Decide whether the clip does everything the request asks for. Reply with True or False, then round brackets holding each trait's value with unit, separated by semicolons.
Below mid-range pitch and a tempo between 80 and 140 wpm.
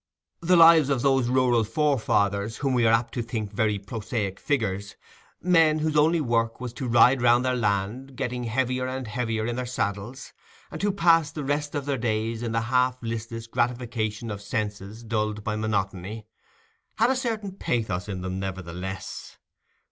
False (120 Hz; 165 wpm)